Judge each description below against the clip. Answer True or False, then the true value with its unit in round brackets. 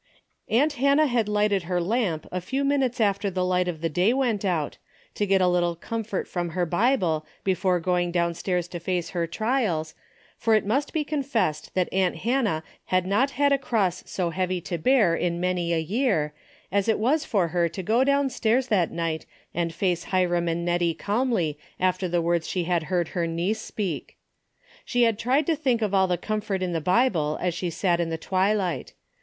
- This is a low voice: False (185 Hz)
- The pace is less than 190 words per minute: False (195 wpm)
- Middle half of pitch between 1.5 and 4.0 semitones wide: False (4.7 semitones)